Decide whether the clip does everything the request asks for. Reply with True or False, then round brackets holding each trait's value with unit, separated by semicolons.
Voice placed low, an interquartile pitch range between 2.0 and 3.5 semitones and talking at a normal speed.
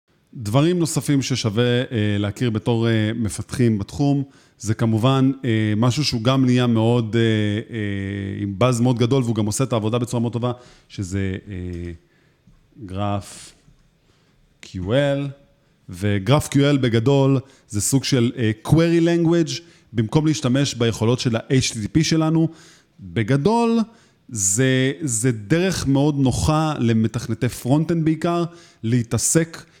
False (125 Hz; 4.3 semitones; 120 wpm)